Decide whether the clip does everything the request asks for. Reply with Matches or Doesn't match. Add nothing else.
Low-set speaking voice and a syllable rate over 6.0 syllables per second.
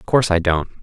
Matches